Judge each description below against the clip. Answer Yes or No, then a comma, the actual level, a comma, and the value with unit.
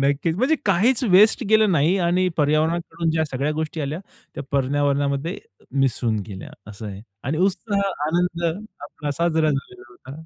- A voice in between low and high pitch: Yes, medium, 155 Hz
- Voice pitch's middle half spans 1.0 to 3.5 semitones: No, average, 4.2 semitones